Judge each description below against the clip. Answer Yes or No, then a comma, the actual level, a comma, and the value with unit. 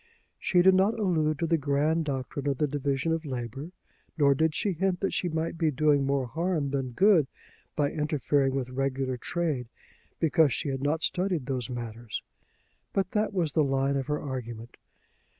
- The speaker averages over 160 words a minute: Yes, average, 180 wpm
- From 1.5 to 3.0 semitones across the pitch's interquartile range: No, average, 3.6 semitones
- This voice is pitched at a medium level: Yes, medium, 145 Hz